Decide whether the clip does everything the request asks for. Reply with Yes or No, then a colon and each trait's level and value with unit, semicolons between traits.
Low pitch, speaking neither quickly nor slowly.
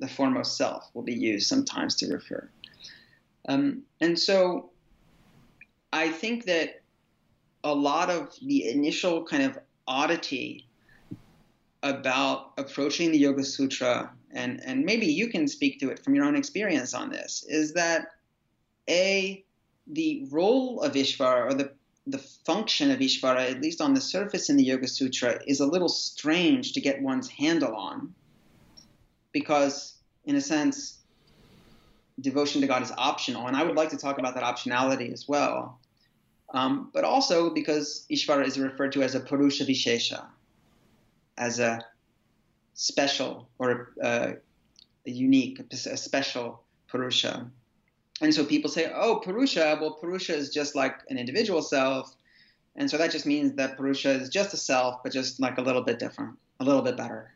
No: medium, 155 Hz; average, 160 wpm